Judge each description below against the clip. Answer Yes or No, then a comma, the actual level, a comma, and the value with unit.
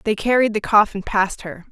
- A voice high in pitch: Yes, high, 210 Hz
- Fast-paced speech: Yes, fast, 210 wpm